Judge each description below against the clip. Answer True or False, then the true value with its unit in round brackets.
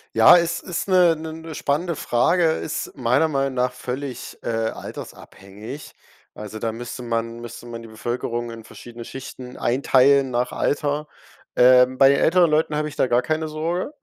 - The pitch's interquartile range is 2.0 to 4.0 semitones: False (4.5 semitones)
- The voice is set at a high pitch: False (130 Hz)